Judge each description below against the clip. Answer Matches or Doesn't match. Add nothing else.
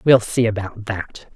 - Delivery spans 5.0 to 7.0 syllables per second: Doesn't match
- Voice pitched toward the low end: Matches